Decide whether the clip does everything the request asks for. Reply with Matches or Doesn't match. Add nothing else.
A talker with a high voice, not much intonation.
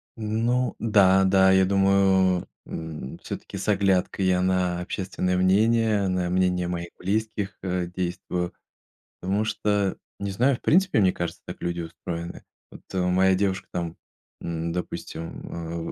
Doesn't match